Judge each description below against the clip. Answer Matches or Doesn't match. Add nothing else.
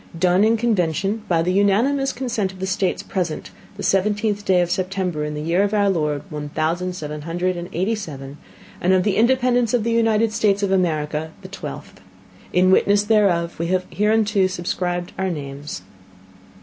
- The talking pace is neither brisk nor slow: Matches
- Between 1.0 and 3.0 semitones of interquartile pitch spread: Doesn't match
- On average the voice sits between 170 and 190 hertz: Matches